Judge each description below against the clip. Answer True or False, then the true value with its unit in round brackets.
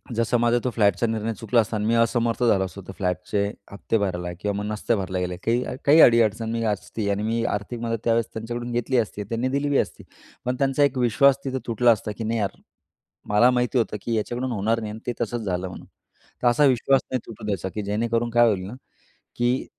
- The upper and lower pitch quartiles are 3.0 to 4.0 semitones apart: False (2.6 semitones)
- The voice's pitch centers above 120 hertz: False (115 Hz)